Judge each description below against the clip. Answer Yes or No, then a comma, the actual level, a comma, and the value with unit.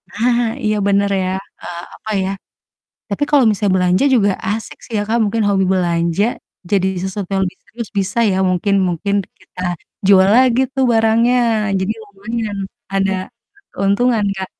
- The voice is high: Yes, high, 200 Hz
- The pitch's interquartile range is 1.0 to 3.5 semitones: Yes, average, 2.8 semitones